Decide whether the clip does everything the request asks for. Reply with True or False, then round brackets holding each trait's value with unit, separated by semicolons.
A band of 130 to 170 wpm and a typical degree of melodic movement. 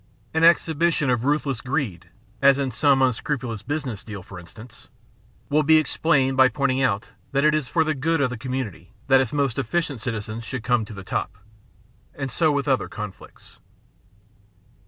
False (185 wpm; 4.4 semitones)